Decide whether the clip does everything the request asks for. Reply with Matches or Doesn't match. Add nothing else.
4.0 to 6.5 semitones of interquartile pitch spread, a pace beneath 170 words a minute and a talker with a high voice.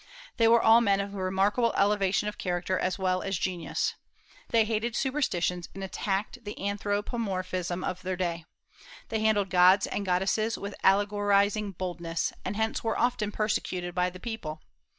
Doesn't match